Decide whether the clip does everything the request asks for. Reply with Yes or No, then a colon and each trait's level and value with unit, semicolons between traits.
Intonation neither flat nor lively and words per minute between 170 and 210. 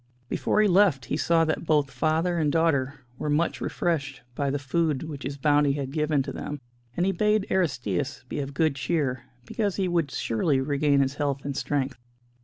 Yes: average, 3.2 semitones; average, 195 wpm